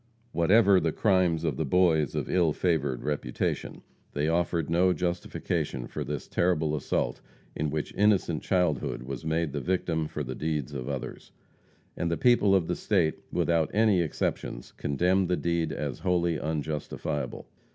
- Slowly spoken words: No, average, 155 wpm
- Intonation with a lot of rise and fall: No, average, 3.3 semitones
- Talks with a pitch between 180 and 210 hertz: No, very low, 80 Hz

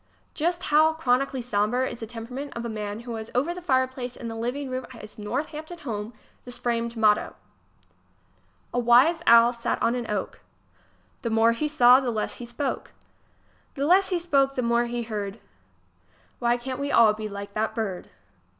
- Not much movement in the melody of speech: No, average, 3.4 semitones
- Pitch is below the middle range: No, high, 240 Hz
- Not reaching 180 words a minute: No, average, 185 wpm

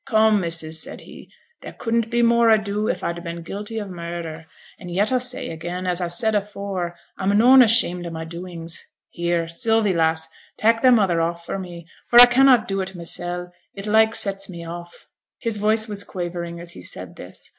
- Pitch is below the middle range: No, medium, 185 Hz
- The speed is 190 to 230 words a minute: Yes, average, 195 wpm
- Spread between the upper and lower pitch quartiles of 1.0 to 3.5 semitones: No, average, 4.3 semitones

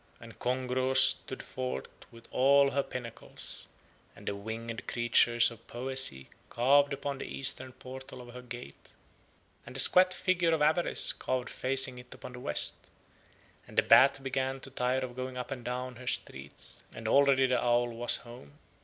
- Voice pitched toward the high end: No, low, 125 Hz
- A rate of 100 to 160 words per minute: No, average, 170 wpm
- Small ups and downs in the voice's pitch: Yes, narrow, 1.9 semitones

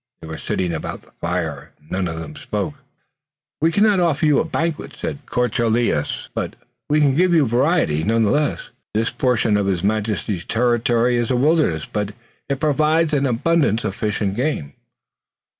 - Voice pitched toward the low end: Yes, low, 120 Hz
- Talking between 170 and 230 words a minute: Yes, average, 180 wpm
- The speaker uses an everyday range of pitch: No, wide, 7.2 semitones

